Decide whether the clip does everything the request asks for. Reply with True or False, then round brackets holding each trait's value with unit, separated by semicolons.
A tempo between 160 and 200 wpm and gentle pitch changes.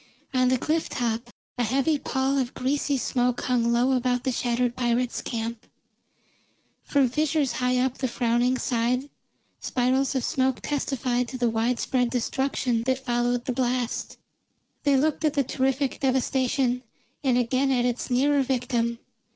False (150 wpm; 1.8 semitones)